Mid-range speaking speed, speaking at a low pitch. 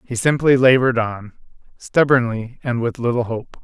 Yes: average, 150 wpm; low, 120 Hz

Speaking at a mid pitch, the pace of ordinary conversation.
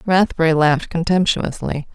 No: medium, 165 Hz; slow, 95 wpm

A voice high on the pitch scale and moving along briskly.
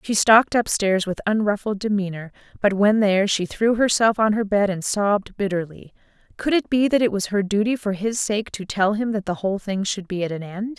Yes: high, 205 Hz; fast, 230 wpm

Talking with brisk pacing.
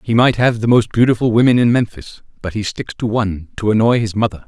Yes: fast, 240 wpm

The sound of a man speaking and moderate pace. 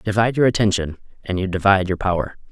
Yes: male; average, 190 wpm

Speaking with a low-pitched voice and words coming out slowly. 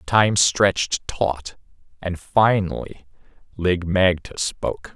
Yes: very low, 90 Hz; slow, 95 wpm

